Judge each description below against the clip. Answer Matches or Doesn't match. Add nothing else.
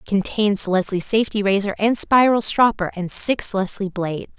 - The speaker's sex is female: Matches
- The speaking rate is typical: Matches